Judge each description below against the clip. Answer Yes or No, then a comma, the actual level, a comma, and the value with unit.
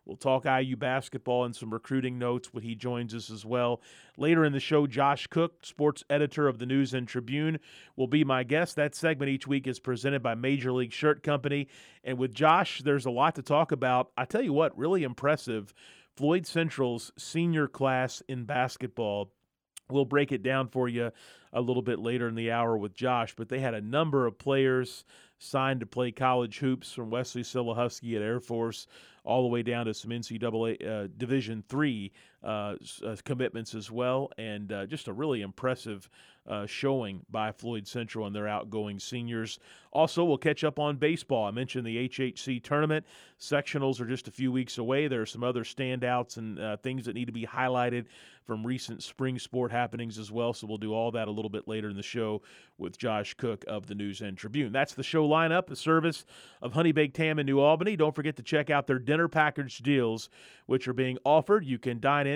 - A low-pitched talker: Yes, low, 125 Hz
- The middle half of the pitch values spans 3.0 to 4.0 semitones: Yes, average, 3.5 semitones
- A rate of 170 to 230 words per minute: Yes, fast, 205 wpm